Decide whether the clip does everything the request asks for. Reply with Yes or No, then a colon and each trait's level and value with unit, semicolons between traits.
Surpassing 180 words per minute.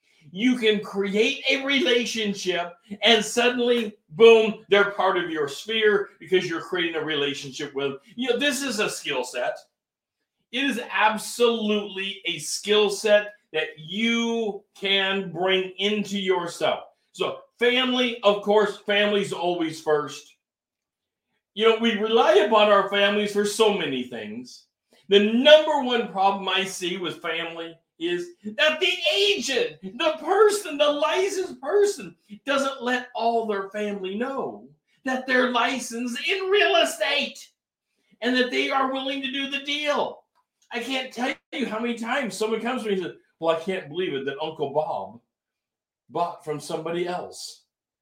No: average, 150 wpm